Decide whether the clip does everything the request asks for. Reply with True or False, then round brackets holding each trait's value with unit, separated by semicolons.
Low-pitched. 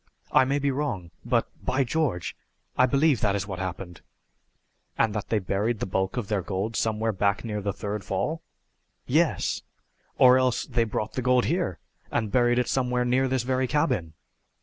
True (115 Hz)